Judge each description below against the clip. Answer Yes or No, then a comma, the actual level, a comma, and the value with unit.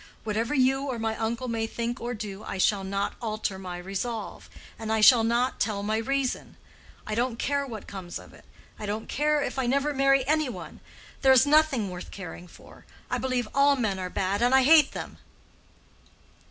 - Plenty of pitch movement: No, average, 4.3 semitones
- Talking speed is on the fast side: No, average, 195 wpm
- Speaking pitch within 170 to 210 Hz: No, high, 230 Hz